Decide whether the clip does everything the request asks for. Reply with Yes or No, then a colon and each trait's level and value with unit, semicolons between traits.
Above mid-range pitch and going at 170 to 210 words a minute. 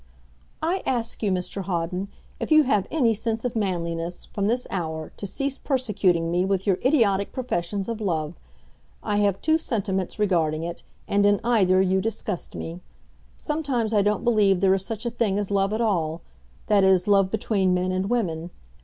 Yes: high, 200 Hz; average, 180 wpm